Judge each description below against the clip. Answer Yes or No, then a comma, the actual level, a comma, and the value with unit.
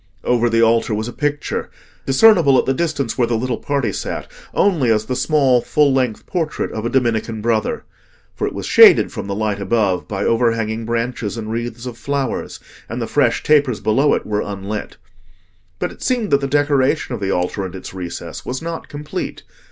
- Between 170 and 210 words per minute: Yes, average, 195 wpm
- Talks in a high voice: No, low, 120 Hz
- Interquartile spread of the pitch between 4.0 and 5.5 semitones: Yes, average, 4.3 semitones